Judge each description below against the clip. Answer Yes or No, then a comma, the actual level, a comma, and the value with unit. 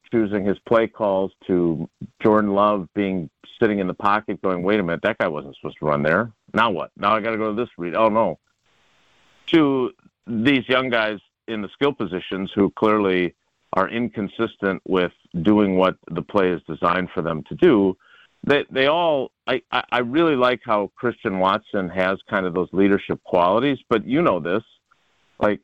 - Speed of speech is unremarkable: Yes, average, 185 wpm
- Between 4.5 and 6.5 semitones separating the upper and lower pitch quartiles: No, average, 3.2 semitones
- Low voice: Yes, low, 100 Hz